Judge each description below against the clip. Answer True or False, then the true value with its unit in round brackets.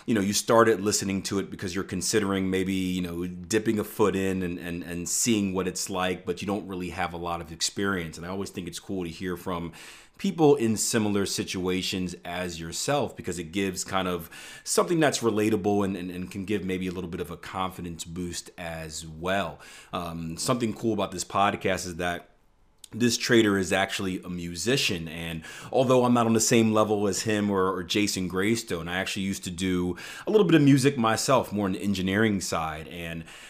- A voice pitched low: True (95 Hz)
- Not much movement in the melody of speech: False (3.2 semitones)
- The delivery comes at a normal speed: False (210 wpm)